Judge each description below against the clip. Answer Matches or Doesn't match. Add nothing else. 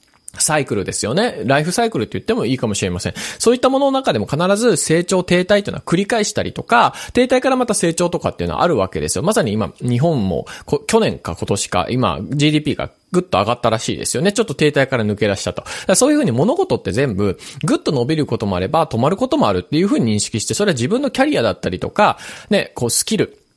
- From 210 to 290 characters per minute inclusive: Doesn't match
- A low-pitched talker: Doesn't match